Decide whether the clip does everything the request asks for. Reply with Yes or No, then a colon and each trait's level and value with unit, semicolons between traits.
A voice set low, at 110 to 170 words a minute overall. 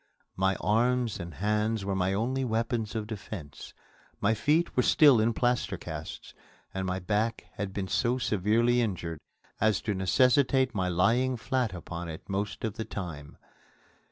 Yes: low, 105 Hz; average, 155 wpm